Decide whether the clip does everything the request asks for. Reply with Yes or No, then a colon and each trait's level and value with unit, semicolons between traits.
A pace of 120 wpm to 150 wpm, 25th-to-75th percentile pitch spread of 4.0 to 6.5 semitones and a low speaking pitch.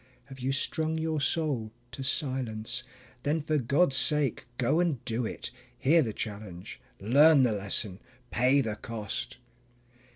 Yes: average, 140 wpm; average, 5.0 semitones; low, 130 Hz